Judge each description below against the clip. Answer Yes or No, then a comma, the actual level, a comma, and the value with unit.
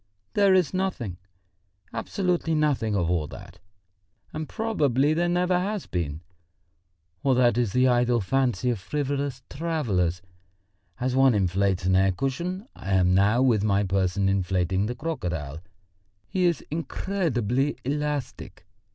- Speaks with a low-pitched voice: Yes, low, 125 Hz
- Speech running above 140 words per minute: No, slow, 135 wpm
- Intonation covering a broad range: Yes, wide, 8.3 semitones